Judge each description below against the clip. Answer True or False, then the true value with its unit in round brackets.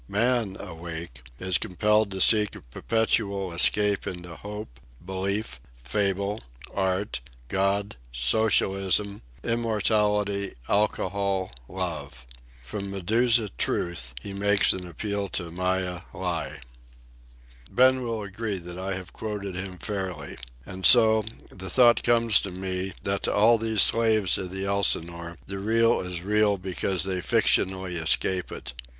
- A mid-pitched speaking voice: False (100 Hz)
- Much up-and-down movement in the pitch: False (2.6 semitones)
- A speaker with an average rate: False (130 wpm)